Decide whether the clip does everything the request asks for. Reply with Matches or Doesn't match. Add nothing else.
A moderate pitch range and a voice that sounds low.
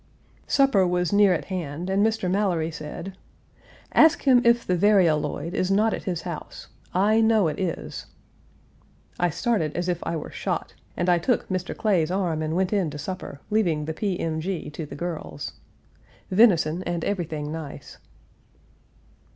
Doesn't match